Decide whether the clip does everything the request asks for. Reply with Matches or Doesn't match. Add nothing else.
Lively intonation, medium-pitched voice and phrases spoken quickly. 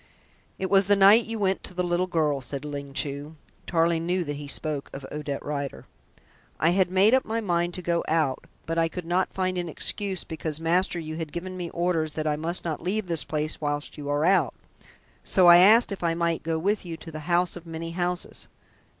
Doesn't match